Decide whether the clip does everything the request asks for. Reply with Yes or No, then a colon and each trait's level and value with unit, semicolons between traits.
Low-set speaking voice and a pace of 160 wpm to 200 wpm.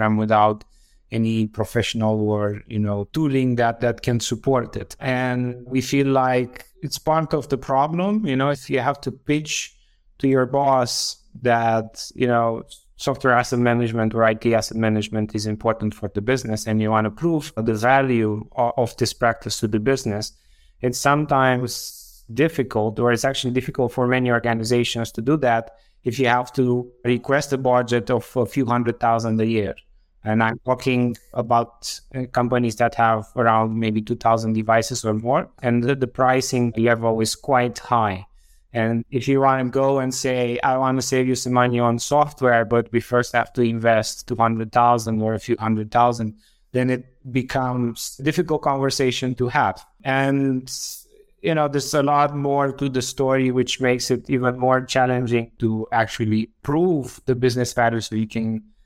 Yes: low, 120 Hz; average, 175 wpm